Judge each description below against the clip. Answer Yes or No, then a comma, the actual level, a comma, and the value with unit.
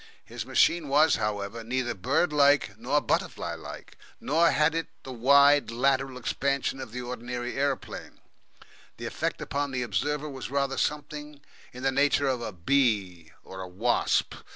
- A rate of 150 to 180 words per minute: Yes, average, 155 wpm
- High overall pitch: No, low, 135 Hz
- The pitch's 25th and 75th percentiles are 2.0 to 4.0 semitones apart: Yes, average, 3.1 semitones